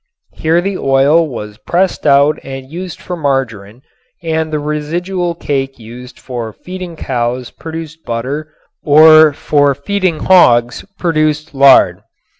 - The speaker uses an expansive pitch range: No, average, 3.7 semitones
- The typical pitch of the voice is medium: Yes, medium, 150 Hz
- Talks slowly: Yes, slow, 125 wpm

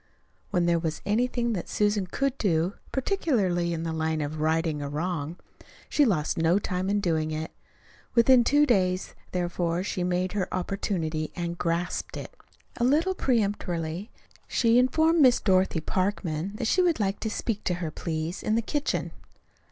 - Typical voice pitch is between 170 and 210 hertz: Yes, medium, 185 Hz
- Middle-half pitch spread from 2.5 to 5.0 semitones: No, wide, 5.5 semitones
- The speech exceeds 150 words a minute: Yes, average, 165 wpm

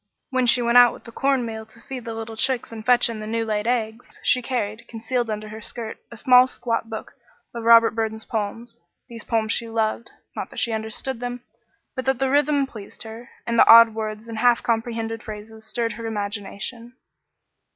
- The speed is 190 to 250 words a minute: Yes, fast, 205 wpm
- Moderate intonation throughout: No, narrow, 1.7 semitones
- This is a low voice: No, high, 230 Hz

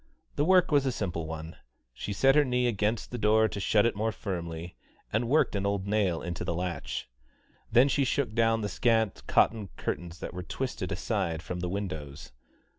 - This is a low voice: Yes, low, 105 Hz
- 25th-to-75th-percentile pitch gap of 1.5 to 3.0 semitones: No, average, 5.0 semitones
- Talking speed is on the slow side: No, average, 190 wpm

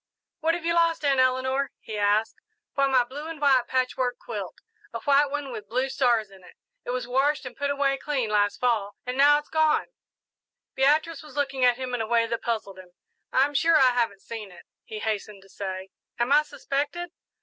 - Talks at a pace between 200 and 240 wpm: Yes, fast, 205 wpm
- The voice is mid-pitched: No, very high, 255 Hz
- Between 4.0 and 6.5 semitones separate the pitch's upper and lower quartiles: Yes, average, 4.3 semitones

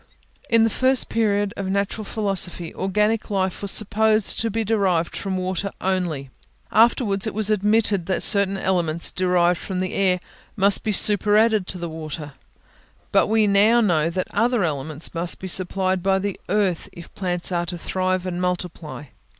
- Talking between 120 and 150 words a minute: No, average, 165 wpm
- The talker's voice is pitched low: No, high, 190 Hz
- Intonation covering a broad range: No, average, 2.9 semitones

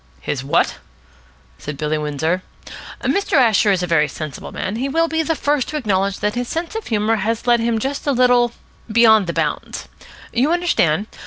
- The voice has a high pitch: Yes, high, 225 Hz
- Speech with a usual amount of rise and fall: No, wide, 7.3 semitones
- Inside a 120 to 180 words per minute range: No, average, 190 wpm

